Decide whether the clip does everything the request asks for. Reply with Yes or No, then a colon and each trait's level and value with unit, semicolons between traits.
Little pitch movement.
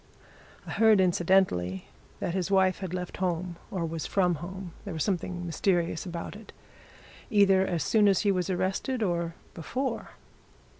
Yes: narrow, 2.3 semitones